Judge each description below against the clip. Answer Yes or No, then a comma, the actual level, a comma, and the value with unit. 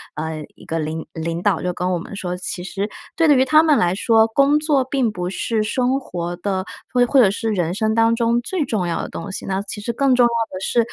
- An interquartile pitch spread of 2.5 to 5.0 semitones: No, wide, 5.5 semitones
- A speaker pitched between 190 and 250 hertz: Yes, high, 215 Hz